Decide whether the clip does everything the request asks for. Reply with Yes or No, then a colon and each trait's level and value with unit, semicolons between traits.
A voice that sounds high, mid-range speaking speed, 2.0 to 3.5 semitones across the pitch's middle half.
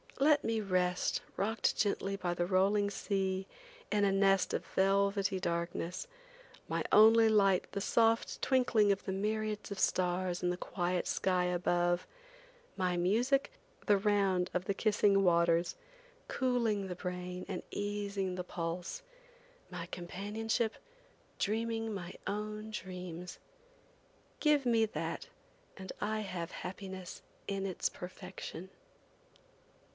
No: high, 195 Hz; slow, 125 wpm; average, 2.9 semitones